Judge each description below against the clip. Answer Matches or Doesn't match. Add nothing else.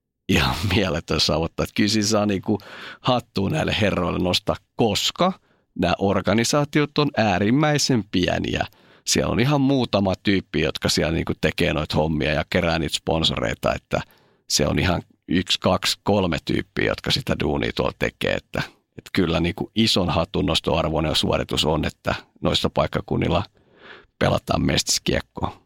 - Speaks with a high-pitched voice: Doesn't match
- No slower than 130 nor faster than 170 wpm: Matches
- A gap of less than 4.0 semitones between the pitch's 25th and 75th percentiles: Doesn't match